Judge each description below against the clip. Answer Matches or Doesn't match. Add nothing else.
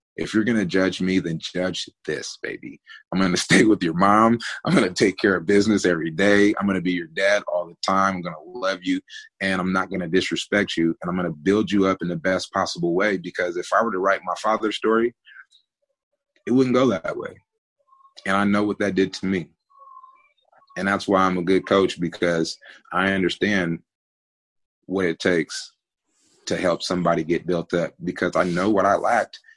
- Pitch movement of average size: Doesn't match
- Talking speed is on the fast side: Matches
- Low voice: Matches